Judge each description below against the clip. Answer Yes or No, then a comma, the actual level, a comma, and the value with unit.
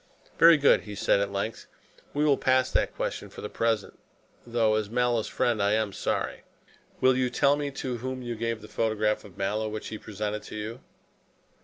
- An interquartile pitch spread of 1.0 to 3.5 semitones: Yes, average, 3.1 semitones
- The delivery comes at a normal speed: Yes, average, 195 wpm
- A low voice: Yes, low, 110 Hz